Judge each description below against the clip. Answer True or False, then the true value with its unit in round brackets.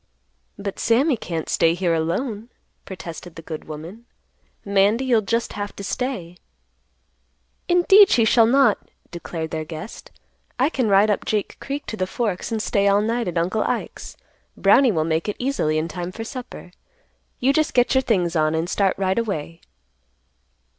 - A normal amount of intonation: False (5.8 semitones)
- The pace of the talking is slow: False (165 wpm)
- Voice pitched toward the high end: True (200 Hz)